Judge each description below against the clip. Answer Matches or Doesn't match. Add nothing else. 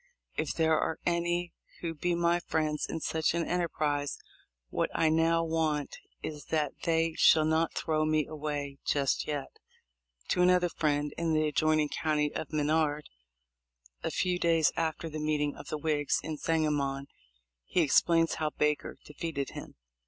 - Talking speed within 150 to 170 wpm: Matches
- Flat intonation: Matches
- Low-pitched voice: Doesn't match